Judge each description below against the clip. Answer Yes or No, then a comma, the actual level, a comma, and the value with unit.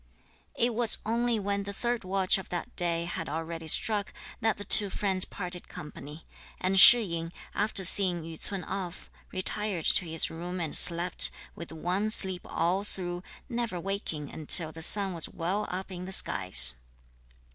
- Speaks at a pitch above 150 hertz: Yes, medium, 185 Hz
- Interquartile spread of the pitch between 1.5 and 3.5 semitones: Yes, average, 3.2 semitones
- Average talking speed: Yes, average, 170 wpm